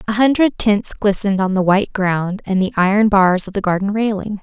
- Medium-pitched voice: No, high, 200 Hz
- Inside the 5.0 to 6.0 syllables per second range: Yes, 5.5 syllables/s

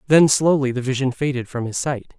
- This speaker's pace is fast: Yes, fast, 220 wpm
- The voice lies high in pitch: No, low, 135 Hz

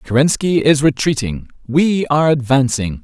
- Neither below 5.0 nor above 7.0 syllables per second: No, 4.7 syllables/s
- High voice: No, medium, 140 Hz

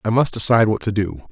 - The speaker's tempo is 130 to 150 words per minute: No, fast, 275 wpm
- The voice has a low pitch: Yes, low, 105 Hz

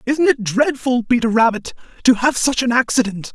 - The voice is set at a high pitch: Yes, high, 235 Hz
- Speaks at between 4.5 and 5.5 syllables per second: Yes, 5.1 syllables/s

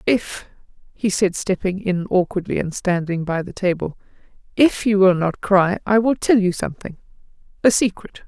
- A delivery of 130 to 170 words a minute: Yes, average, 160 wpm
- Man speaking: No, female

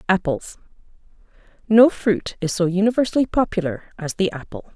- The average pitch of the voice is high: Yes, high, 195 Hz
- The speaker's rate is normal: No, slow, 115 wpm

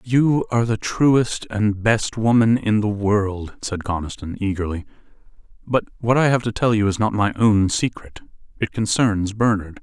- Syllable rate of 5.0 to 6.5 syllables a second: No, 4.5 syllables/s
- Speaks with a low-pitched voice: Yes, low, 105 Hz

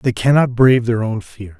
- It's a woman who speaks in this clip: No, male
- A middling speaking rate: No, fast, 225 wpm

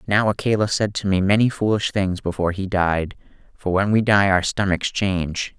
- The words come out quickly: No, average, 195 wpm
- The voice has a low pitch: Yes, low, 100 Hz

